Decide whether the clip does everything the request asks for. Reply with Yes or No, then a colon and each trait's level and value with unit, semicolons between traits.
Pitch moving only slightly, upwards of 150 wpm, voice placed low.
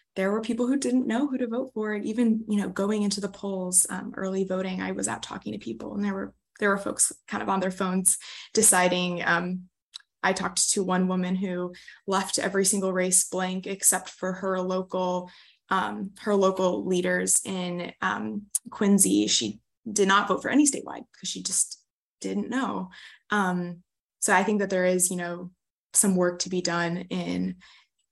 No: narrow, 2.2 semitones; average, 190 wpm; medium, 185 Hz